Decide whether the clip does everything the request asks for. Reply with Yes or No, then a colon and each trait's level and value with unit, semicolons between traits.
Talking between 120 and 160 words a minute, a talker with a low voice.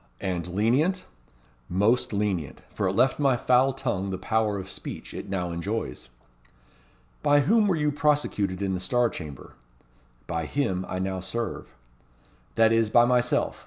Yes: average, 155 wpm; low, 110 Hz